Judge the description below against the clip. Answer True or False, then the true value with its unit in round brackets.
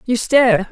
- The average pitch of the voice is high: True (240 Hz)